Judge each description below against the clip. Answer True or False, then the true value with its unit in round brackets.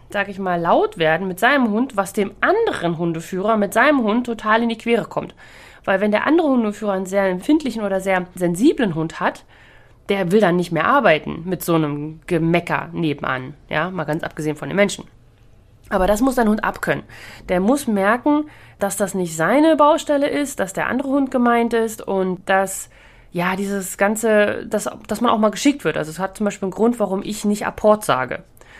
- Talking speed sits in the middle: False (200 wpm)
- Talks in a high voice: True (200 Hz)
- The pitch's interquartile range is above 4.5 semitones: True (5.0 semitones)